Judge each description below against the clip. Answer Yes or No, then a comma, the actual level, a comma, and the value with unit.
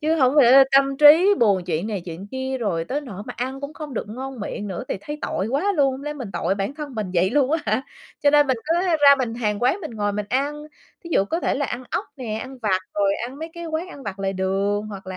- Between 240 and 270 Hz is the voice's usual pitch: Yes, very high, 255 Hz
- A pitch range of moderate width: No, wide, 6.2 semitones